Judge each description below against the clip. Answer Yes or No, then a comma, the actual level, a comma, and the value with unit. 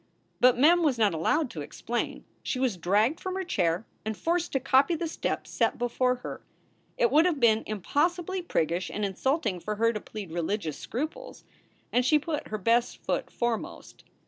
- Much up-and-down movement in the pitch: Yes, wide, 6.9 semitones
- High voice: Yes, high, 245 Hz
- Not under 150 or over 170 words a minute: No, average, 180 wpm